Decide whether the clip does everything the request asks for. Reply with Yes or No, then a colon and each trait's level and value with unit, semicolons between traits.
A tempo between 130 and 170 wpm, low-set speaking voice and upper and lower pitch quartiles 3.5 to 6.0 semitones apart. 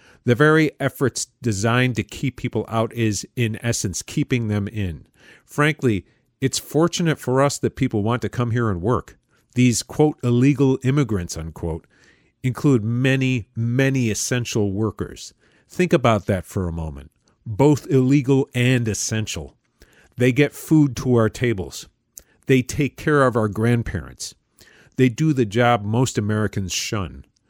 Yes: average, 145 wpm; low, 120 Hz; average, 3.8 semitones